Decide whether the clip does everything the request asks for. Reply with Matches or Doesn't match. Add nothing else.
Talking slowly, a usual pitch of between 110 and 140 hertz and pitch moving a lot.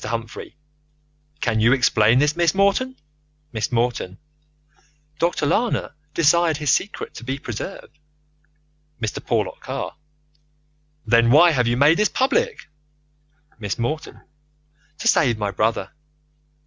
Matches